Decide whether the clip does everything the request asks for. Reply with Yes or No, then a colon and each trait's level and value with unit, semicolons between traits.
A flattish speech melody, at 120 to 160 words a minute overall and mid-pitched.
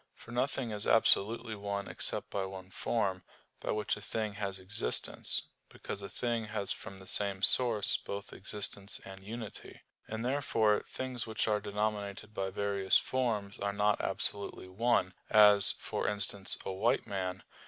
No: narrow, 2.0 semitones; average, 155 wpm; low, 105 Hz